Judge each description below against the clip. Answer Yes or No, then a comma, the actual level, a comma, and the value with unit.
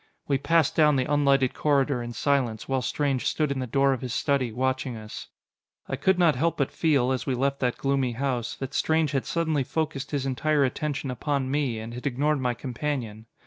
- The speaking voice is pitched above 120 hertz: Yes, low, 135 Hz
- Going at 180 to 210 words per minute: Yes, fast, 205 wpm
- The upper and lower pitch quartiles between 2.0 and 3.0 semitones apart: Yes, narrow, 2.6 semitones